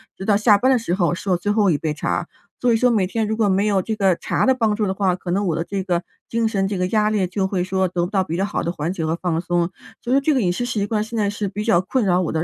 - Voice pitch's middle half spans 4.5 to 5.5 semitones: No, average, 3.2 semitones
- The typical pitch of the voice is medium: No, high, 195 Hz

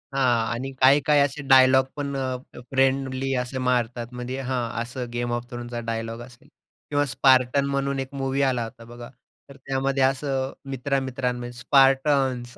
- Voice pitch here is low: Yes, low, 130 Hz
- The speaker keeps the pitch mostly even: Yes, narrow, 1.8 semitones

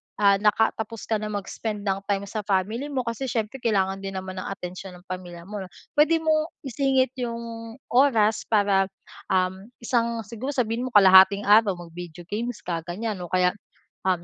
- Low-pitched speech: No, high, 210 Hz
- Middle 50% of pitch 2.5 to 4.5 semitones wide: Yes, average, 3.5 semitones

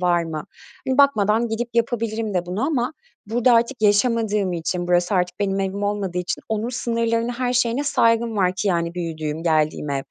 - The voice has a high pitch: Yes, high, 210 Hz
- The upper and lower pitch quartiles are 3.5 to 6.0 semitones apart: Yes, average, 4.7 semitones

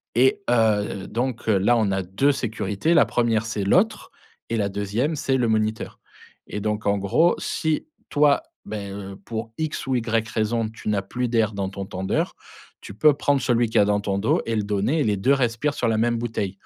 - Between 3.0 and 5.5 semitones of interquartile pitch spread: Yes, average, 3.4 semitones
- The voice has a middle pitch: No, low, 110 Hz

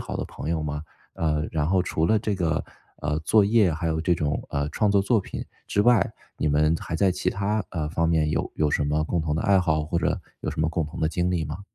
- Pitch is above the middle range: No, very low, 80 Hz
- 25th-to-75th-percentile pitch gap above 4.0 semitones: No, average, 3.6 semitones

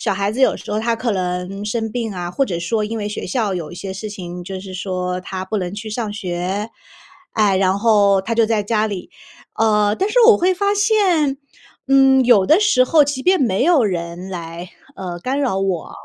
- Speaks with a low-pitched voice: No, high, 210 Hz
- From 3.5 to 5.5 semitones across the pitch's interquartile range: Yes, average, 5.0 semitones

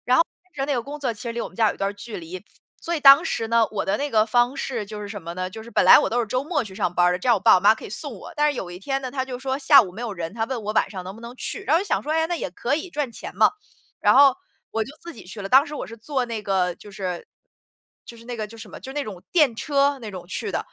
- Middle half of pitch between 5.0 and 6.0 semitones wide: Yes, average, 5.3 semitones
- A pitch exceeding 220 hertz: Yes, high, 235 Hz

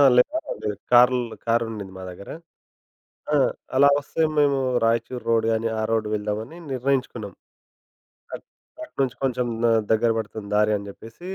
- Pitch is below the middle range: Yes, low, 115 Hz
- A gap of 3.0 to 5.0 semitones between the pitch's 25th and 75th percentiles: No, narrow, 2.6 semitones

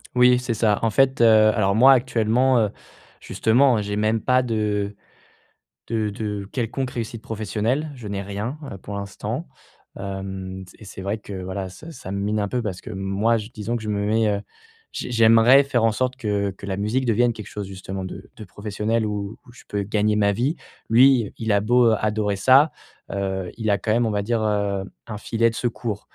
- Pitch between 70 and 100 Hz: No, low, 110 Hz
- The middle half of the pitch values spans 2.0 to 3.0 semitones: Yes, narrow, 2.6 semitones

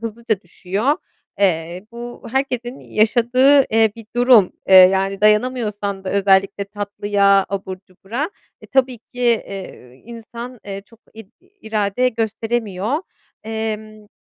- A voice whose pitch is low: No, high, 220 Hz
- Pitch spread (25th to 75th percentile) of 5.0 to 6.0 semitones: No, average, 3.3 semitones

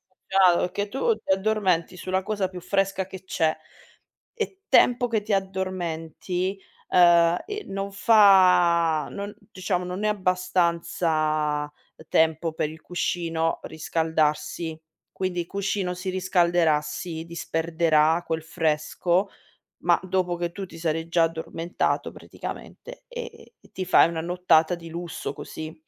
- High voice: No, medium, 175 Hz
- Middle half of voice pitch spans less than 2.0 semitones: No, average, 2.7 semitones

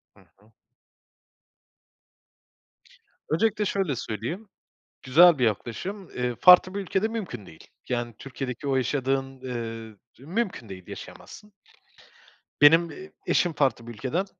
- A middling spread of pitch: No, wide, 7.4 semitones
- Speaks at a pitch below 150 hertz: Yes, low, 135 Hz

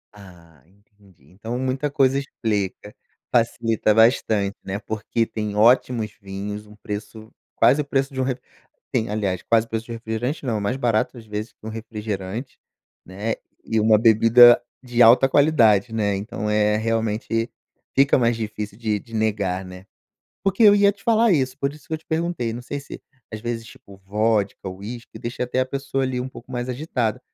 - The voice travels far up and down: No, average, 3.4 semitones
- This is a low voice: Yes, low, 115 Hz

